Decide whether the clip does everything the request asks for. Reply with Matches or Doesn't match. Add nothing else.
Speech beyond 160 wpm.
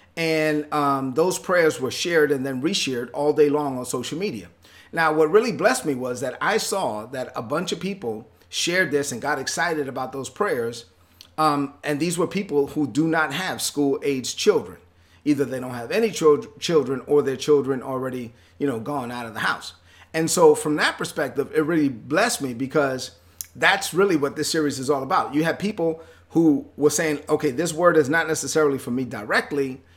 Matches